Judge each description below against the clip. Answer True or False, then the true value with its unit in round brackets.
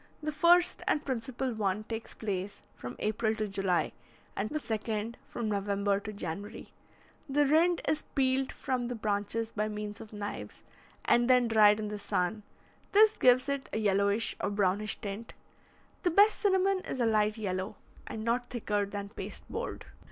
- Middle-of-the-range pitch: False (220 Hz)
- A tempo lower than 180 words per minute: True (165 wpm)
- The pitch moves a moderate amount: True (3.9 semitones)